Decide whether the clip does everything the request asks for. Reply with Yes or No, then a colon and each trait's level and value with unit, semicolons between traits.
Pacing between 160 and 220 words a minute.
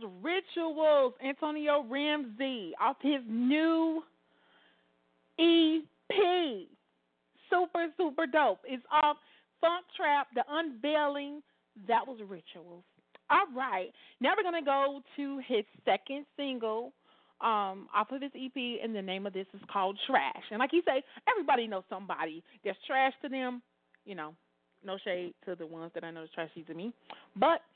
No: average, 145 wpm